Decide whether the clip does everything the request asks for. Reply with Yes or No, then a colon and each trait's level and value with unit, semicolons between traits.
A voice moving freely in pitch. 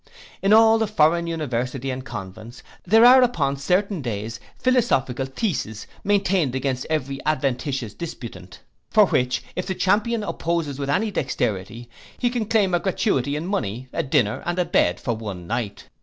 Yes: wide, 8.1 semitones